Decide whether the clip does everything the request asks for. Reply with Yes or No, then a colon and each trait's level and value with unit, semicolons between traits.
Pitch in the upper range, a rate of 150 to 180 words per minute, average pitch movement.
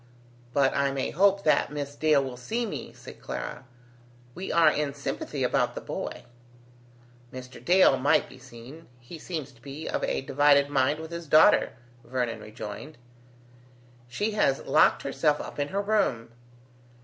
No: medium, 145 Hz; average, 160 wpm; average, 3.8 semitones